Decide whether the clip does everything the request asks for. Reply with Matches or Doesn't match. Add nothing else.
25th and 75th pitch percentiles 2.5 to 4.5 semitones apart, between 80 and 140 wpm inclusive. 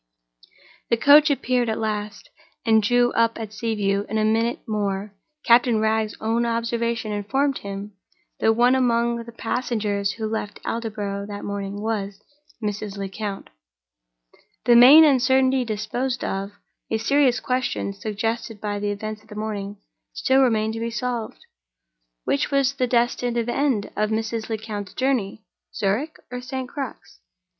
Matches